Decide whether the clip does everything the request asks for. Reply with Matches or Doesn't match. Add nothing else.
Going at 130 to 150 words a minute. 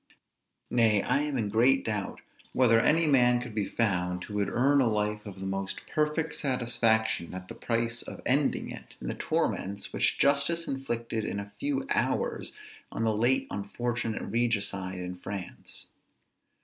Doesn't match